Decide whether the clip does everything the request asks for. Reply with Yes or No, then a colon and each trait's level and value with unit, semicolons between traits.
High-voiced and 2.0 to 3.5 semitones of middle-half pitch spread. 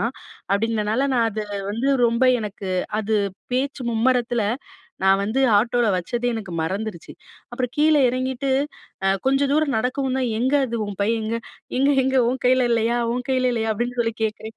Yes: high, 235 Hz; average, 3.0 semitones